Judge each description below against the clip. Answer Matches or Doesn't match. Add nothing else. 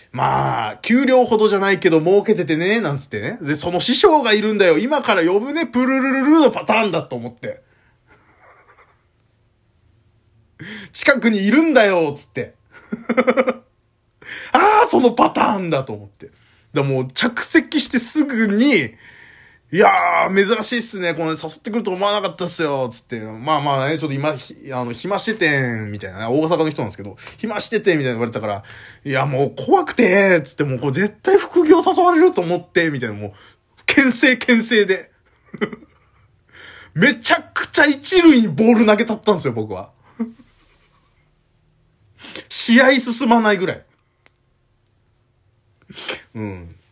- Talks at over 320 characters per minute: Doesn't match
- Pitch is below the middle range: Doesn't match